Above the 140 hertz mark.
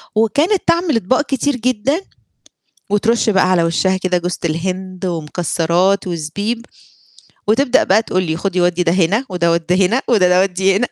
Yes: high, 190 Hz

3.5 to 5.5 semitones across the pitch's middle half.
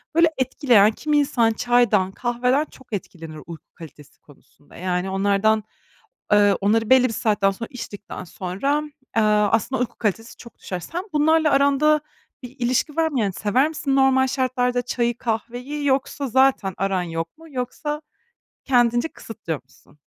Yes: average, 5.2 semitones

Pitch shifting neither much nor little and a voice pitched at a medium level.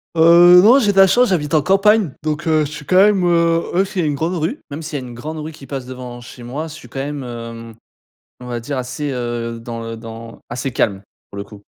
No: wide, 5.8 semitones; medium, 145 Hz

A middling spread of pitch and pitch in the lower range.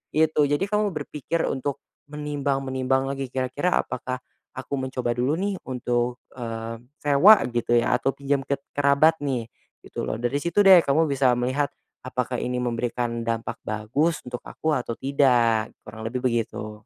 Yes: average, 3.3 semitones; low, 130 Hz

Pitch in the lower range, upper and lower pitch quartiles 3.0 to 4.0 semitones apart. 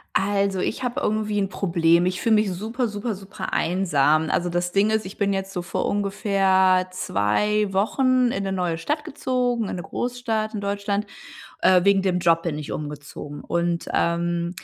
No: high, 195 Hz; average, 3.4 semitones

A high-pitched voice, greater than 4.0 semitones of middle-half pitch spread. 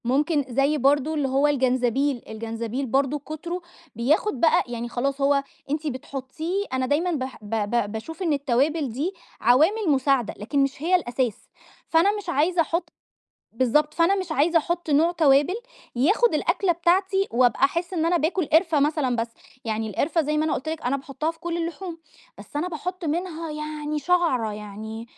Yes: very high, 295 Hz; average, 4.6 semitones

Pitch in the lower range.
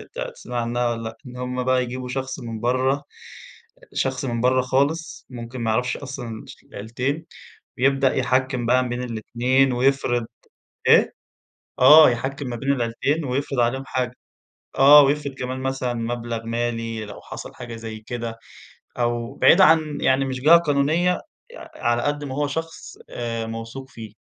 Yes: low, 125 Hz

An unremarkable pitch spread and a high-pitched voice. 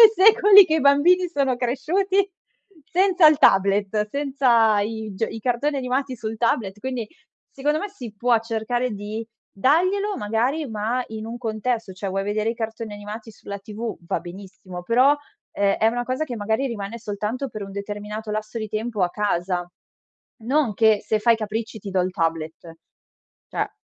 Yes: average, 4.3 semitones; high, 225 Hz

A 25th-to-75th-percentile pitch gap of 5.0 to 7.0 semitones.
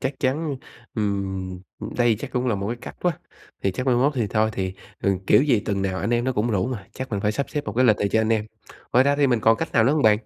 No: average, 4.3 semitones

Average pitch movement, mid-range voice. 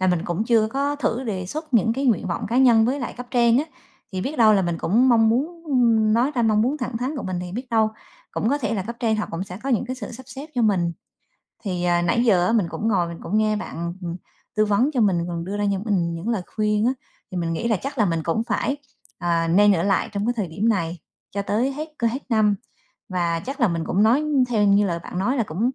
No: average, 4.9 semitones; high, 215 Hz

